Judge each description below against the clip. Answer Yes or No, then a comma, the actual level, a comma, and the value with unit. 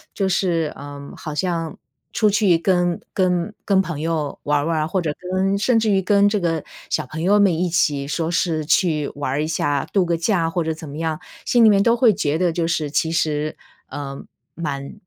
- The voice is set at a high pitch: No, medium, 165 Hz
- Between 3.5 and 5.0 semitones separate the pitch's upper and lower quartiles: Yes, average, 3.8 semitones